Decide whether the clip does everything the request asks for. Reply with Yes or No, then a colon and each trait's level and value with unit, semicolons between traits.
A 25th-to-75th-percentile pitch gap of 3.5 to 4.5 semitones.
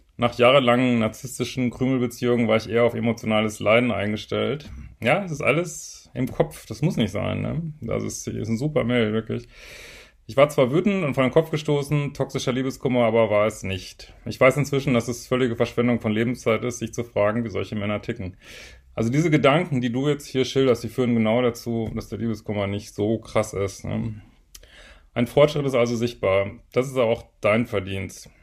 No: average, 2.9 semitones